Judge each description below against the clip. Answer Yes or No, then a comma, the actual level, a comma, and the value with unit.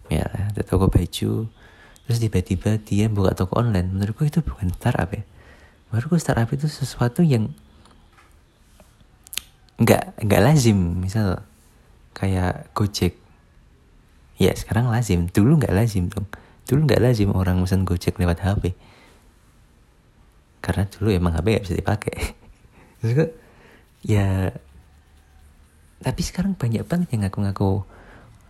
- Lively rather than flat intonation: No, average, 4.3 semitones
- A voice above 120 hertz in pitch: No, low, 100 Hz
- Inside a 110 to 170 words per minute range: Yes, average, 120 wpm